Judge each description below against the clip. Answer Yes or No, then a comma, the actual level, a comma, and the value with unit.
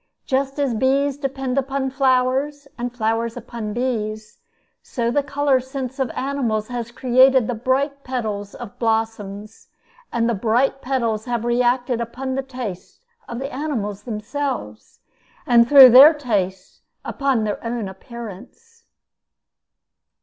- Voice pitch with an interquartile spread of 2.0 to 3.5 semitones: Yes, average, 3.1 semitones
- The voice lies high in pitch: Yes, high, 245 Hz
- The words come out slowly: Yes, slow, 130 wpm